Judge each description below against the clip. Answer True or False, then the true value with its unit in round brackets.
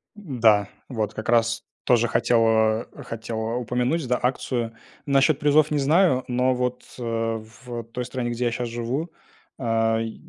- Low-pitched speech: True (120 Hz)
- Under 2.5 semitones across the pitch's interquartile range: True (2.1 semitones)